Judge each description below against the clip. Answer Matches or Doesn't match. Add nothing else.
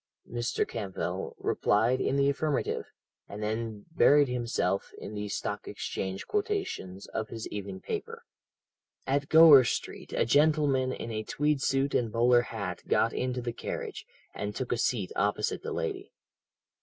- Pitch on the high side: Doesn't match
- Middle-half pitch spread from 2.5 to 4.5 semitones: Doesn't match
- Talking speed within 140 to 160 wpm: Matches